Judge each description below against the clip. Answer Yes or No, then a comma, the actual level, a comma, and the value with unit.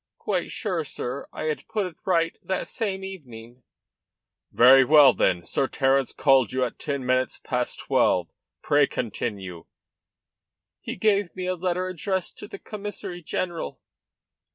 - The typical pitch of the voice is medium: Yes, medium, 150 Hz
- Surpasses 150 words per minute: No, average, 145 wpm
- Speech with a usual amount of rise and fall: No, wide, 6.6 semitones